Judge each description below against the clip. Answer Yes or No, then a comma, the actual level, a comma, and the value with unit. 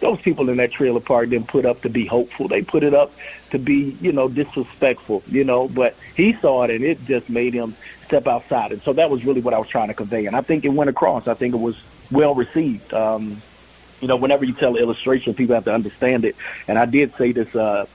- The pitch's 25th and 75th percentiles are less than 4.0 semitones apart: Yes, average, 3.0 semitones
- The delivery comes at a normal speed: No, fast, 255 wpm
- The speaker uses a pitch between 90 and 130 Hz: Yes, low, 125 Hz